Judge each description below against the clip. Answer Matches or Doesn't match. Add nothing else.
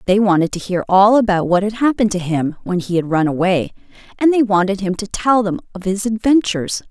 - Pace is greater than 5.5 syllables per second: Matches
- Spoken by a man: Doesn't match